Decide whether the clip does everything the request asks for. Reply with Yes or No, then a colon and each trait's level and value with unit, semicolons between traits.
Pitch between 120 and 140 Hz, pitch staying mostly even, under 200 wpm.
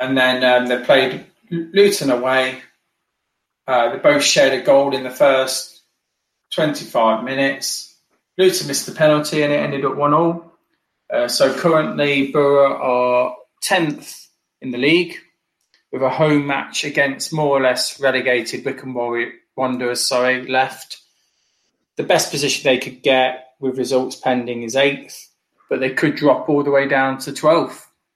Yes: low, 135 Hz; narrow, 2.3 semitones; average, 150 wpm